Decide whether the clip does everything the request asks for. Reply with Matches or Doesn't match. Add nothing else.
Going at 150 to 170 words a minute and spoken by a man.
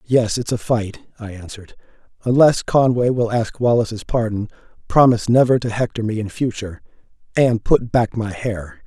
Matches